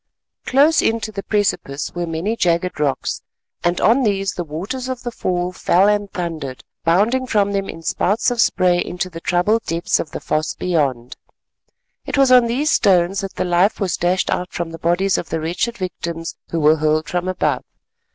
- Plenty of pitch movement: No, average, 3.9 semitones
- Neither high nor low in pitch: Yes, medium, 180 Hz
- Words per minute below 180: No, average, 190 wpm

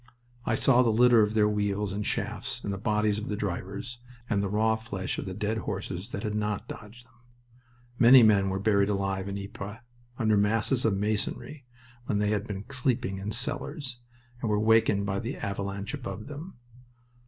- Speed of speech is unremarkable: Yes, average, 190 wpm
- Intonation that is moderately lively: No, narrow, 2.3 semitones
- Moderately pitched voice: No, low, 105 Hz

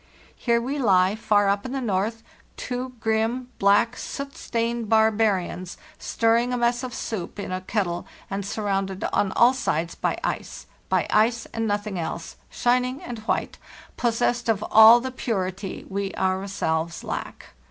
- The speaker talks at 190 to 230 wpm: No, average, 150 wpm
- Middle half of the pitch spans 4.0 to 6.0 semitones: No, average, 3.6 semitones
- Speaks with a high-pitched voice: Yes, high, 220 Hz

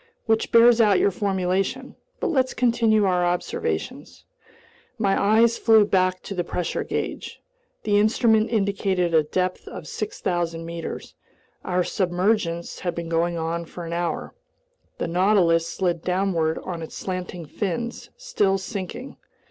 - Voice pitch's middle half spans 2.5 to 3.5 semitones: No, average, 4.0 semitones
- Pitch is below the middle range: No, medium, 185 Hz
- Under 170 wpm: Yes, average, 140 wpm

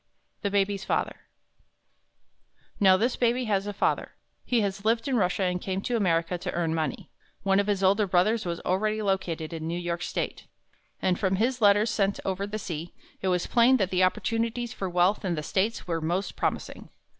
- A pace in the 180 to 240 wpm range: Yes, average, 190 wpm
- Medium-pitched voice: No, high, 195 Hz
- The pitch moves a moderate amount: Yes, average, 3.1 semitones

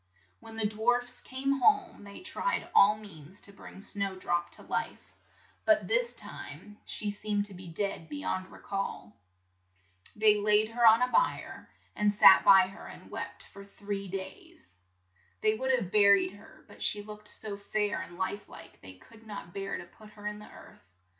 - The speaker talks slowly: No, average, 185 wpm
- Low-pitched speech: No, high, 205 Hz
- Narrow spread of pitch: Yes, narrow, 2.0 semitones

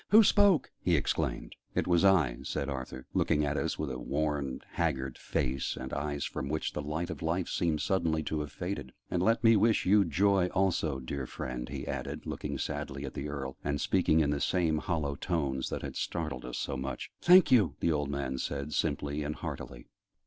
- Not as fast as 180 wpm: No, average, 200 wpm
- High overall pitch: No, very low, 75 Hz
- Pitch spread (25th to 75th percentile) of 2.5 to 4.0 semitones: No, average, 4.4 semitones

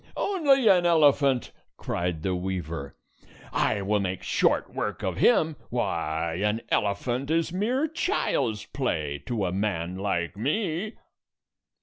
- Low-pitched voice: Yes, low, 110 Hz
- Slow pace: Yes, slow, 125 wpm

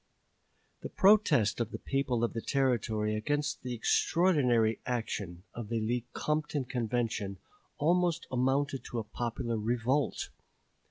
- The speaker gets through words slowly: Yes, slow, 120 wpm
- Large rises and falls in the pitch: No, average, 4.1 semitones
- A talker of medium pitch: No, low, 120 Hz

